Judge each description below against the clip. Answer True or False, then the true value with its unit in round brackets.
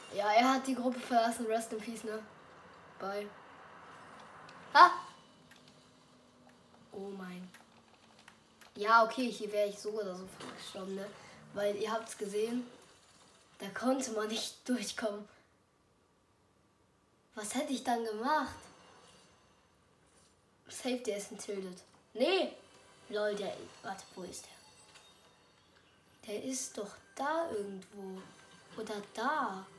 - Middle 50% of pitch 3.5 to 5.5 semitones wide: False (2.8 semitones)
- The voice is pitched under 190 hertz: False (215 Hz)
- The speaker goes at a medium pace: False (110 wpm)